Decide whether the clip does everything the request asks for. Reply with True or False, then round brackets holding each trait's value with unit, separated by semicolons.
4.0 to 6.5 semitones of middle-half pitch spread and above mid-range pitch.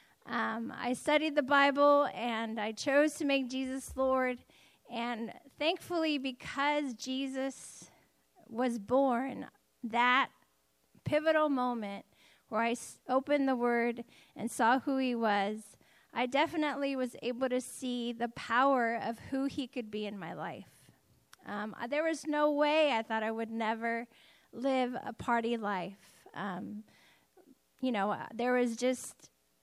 False (3.3 semitones; 250 Hz)